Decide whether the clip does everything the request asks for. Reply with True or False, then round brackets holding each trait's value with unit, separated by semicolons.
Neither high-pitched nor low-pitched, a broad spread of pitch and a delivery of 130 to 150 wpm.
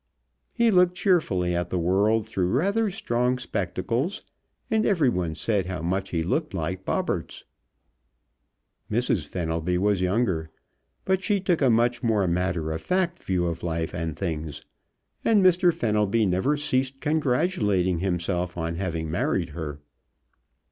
False (95 Hz; 8.5 semitones; 140 wpm)